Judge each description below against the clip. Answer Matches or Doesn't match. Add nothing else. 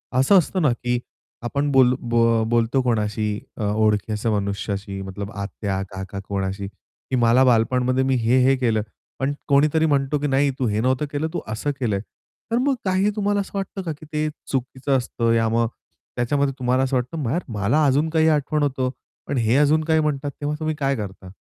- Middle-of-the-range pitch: Doesn't match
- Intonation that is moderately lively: Matches